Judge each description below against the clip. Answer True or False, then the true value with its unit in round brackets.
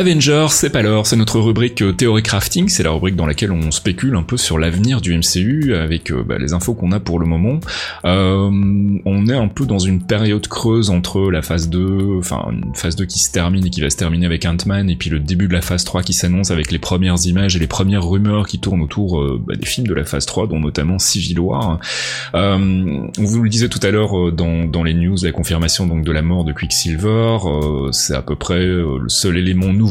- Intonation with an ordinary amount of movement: True (3.7 semitones)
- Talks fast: True (245 wpm)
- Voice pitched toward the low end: True (90 Hz)